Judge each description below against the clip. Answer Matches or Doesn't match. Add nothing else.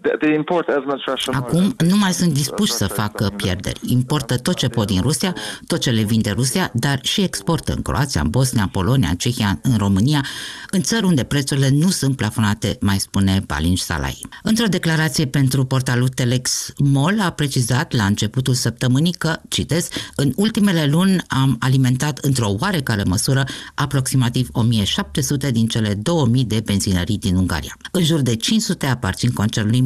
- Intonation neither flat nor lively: Doesn't match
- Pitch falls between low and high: Doesn't match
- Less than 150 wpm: Doesn't match